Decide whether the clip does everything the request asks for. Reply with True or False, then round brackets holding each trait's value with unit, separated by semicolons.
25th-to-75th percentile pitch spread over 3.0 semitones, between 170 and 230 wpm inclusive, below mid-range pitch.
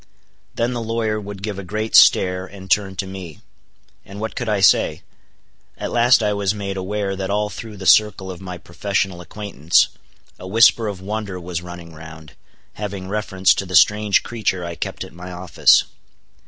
False (2.6 semitones; 180 wpm; 95 Hz)